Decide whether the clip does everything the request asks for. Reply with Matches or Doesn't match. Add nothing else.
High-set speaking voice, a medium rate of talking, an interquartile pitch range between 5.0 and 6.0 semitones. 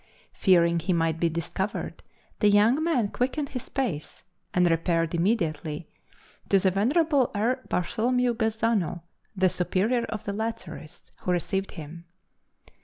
Doesn't match